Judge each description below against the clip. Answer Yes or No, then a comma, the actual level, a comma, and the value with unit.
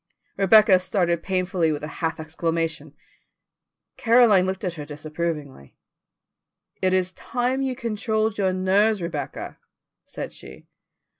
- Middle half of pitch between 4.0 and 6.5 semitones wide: Yes, average, 4.6 semitones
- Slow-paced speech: Yes, slow, 120 wpm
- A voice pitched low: No, medium, 185 Hz